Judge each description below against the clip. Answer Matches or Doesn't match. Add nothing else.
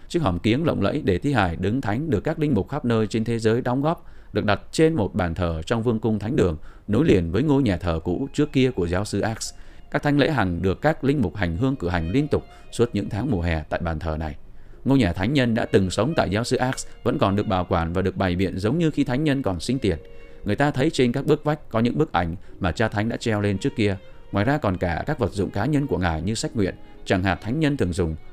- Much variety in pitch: Matches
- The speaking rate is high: Matches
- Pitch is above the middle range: Doesn't match